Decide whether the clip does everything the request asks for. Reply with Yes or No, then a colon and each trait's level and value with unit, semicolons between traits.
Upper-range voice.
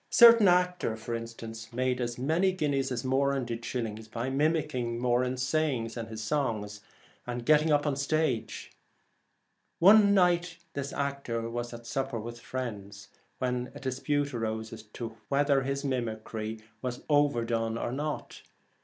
No: low, 125 Hz